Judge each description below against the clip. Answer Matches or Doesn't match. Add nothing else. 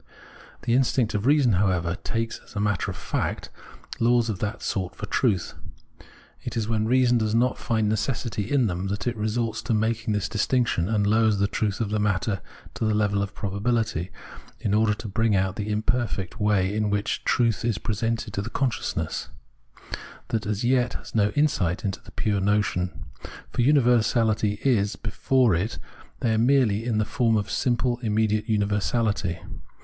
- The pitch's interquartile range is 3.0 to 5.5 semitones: Doesn't match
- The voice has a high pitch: Doesn't match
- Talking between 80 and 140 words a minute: Doesn't match